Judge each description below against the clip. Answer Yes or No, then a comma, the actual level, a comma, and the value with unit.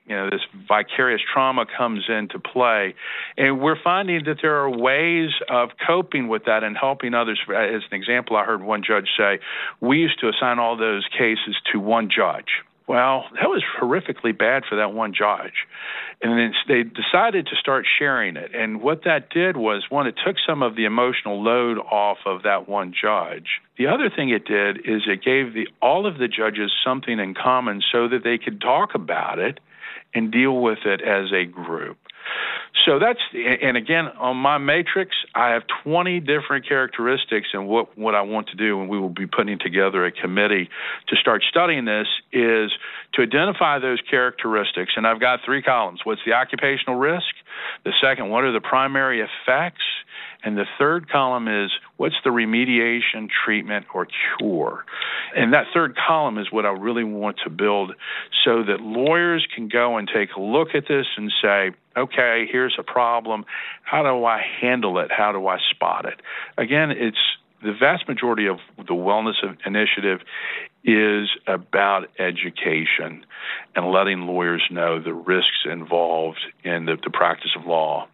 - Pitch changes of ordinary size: Yes, average, 3.9 semitones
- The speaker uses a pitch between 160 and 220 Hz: No, low, 115 Hz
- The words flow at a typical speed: Yes, average, 175 wpm